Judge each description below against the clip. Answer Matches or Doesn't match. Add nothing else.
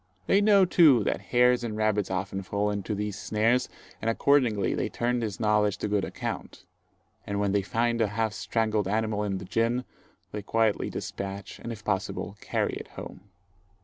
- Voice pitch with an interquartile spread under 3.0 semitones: Matches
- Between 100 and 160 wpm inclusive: Doesn't match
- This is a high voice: Doesn't match